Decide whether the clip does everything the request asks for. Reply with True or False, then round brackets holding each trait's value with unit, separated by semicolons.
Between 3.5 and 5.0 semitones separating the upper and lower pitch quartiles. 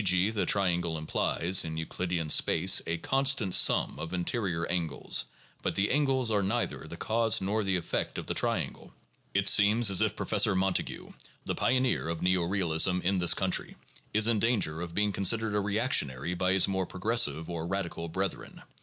True (3.8 semitones)